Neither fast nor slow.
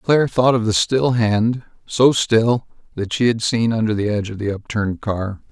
Yes: average, 185 wpm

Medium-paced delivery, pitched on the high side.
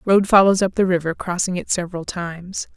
No: average, 195 wpm; medium, 180 Hz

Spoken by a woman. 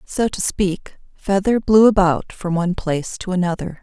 Yes: female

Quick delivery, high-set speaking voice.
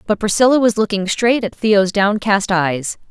No: average, 175 wpm; high, 205 Hz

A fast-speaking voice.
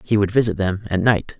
Yes: fast, 260 wpm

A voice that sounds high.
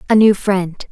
Yes: high, 200 Hz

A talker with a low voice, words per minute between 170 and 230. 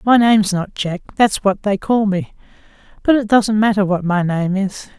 No: high, 205 Hz; fast, 205 wpm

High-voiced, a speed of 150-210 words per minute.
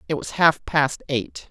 No: medium, 145 Hz; average, 200 wpm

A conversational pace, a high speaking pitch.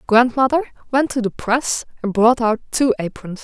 Yes: average, 175 wpm; high, 240 Hz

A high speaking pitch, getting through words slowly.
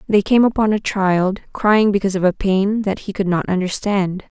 No: high, 200 Hz; fast, 205 wpm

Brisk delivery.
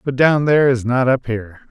Yes: fast, 245 wpm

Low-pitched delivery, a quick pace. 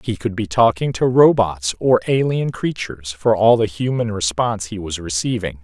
No: low, 105 Hz; average, 180 wpm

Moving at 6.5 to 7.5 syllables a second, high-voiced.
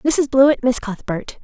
No: 4.4 syllables/s; very high, 255 Hz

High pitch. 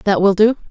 Yes: high, 200 Hz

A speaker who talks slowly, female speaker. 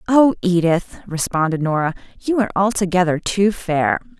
Yes: slow, 130 wpm; female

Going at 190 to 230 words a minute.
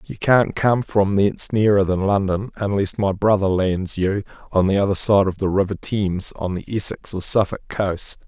Yes: average, 195 wpm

